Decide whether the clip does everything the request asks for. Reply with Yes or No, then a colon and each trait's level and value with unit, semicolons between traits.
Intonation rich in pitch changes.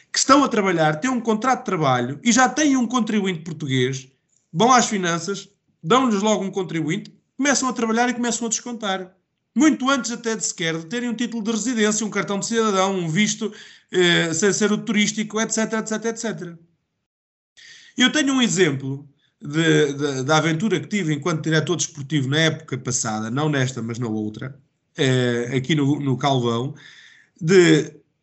Yes: wide, 7.1 semitones